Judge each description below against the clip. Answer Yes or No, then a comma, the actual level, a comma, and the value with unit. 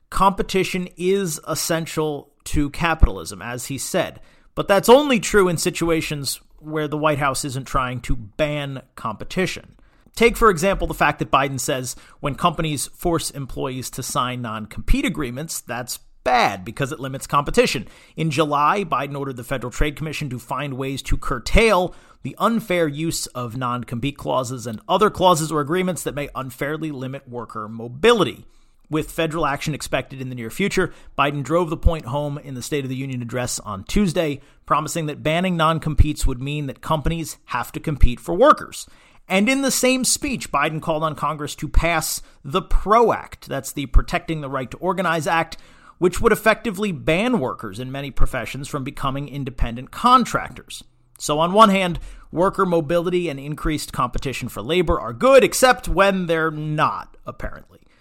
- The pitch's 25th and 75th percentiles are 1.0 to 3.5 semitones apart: No, average, 4.7 semitones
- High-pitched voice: No, medium, 150 Hz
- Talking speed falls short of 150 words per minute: No, average, 170 wpm